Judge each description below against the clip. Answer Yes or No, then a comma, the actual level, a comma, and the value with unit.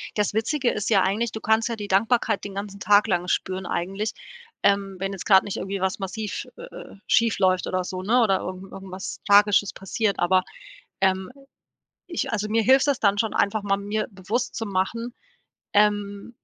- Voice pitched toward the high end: Yes, high, 200 Hz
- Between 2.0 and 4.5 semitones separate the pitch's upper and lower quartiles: Yes, narrow, 2.5 semitones